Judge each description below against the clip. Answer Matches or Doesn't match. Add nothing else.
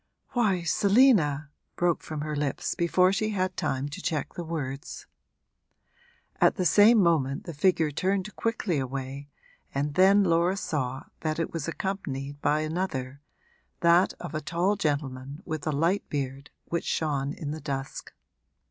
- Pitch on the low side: Doesn't match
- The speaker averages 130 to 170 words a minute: Matches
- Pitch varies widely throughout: Doesn't match